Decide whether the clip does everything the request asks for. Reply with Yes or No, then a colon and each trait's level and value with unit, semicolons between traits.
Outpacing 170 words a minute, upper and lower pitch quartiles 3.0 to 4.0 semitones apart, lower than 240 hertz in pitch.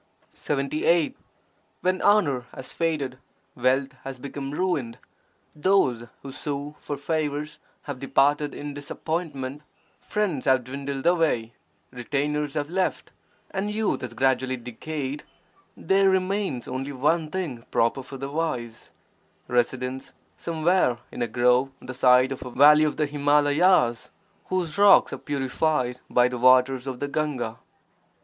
No: slow, 135 wpm; average, 3.6 semitones; medium, 140 Hz